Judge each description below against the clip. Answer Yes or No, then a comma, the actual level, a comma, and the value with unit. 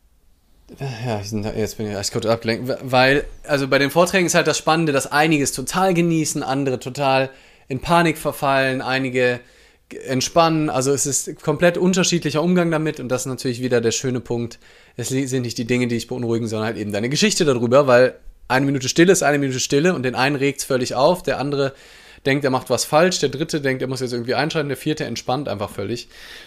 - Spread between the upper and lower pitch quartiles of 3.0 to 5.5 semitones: Yes, average, 3.3 semitones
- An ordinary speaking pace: No, fast, 210 wpm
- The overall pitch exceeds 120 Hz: Yes, low, 135 Hz